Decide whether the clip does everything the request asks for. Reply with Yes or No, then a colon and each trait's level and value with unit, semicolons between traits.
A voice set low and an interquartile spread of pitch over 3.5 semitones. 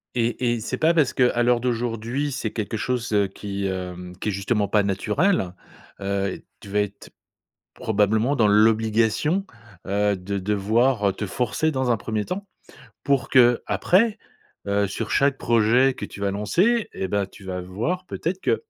Yes: low, 110 Hz; average, 4.2 semitones